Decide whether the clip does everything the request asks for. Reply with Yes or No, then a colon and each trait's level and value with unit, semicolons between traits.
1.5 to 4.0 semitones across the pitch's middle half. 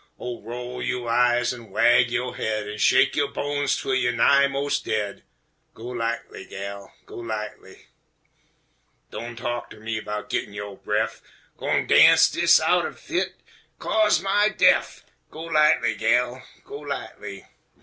Yes: average, 3.5 semitones